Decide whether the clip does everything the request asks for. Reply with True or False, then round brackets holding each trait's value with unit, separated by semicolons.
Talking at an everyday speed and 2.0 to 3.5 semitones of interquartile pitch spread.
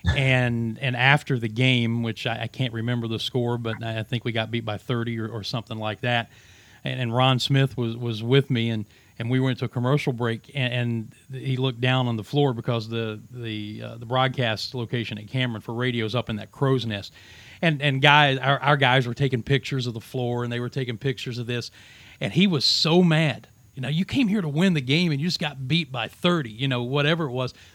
False (240 wpm; 2.9 semitones)